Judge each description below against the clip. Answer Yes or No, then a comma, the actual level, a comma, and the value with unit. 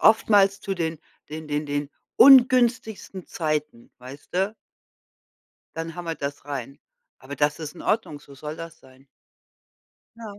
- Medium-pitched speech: Yes, medium, 160 Hz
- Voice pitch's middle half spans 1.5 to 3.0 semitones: No, average, 5.3 semitones